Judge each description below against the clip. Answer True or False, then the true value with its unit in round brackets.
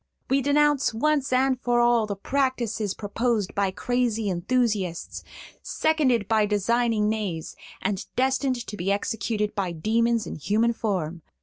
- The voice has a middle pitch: False (225 Hz)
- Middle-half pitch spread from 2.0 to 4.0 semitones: True (3.7 semitones)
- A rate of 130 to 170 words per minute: True (135 wpm)